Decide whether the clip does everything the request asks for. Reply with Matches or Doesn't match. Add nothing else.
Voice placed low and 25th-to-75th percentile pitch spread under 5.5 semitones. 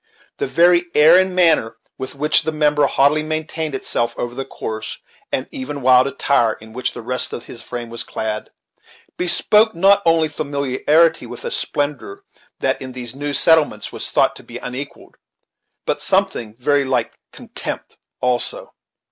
Doesn't match